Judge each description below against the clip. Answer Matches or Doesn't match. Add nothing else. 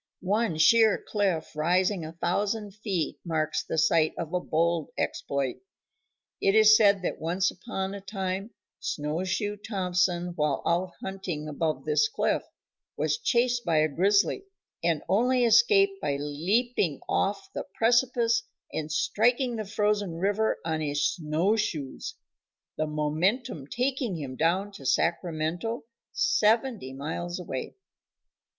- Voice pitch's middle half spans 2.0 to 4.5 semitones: Doesn't match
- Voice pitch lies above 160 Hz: Matches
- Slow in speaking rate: Matches